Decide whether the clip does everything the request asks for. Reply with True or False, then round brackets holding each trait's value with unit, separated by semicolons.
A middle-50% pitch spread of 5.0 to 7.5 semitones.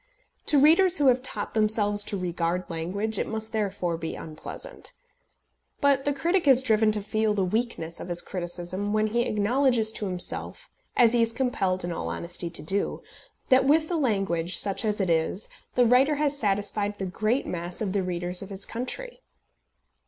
True (5.5 semitones)